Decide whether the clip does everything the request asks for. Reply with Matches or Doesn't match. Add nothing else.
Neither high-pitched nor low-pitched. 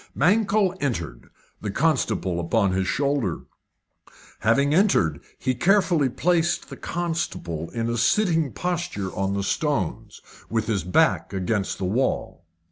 Doesn't match